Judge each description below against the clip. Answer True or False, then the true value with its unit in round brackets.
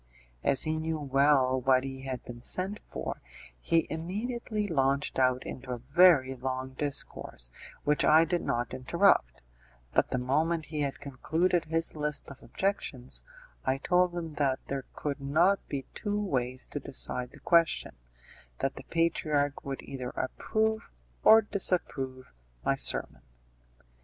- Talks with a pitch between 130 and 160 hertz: True (140 Hz)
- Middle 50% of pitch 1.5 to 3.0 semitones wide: False (4.3 semitones)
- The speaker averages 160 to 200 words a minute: False (145 wpm)